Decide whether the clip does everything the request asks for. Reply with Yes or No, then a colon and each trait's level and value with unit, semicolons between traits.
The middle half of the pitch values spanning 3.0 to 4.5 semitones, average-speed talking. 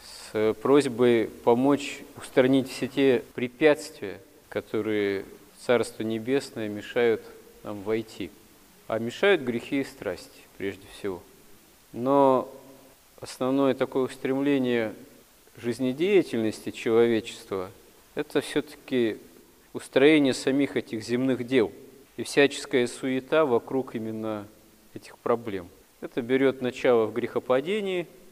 No: average, 3.4 semitones; slow, 95 wpm